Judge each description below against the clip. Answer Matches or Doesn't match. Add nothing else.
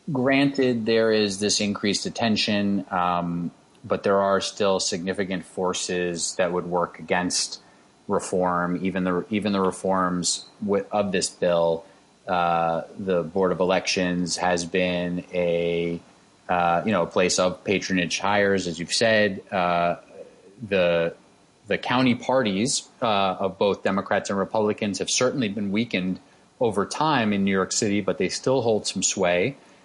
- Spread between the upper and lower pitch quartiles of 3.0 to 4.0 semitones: Doesn't match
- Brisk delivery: Doesn't match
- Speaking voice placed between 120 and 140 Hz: Doesn't match